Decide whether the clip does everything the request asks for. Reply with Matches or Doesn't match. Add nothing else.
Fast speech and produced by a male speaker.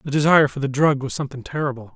Matches